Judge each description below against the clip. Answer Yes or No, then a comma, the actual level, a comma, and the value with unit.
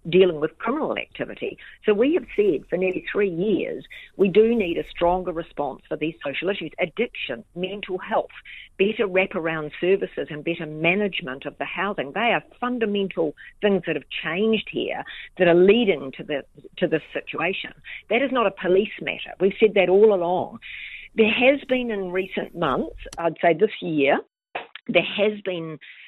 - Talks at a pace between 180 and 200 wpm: No, average, 170 wpm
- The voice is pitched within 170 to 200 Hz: Yes, high, 190 Hz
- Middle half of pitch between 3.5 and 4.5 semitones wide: Yes, average, 4.2 semitones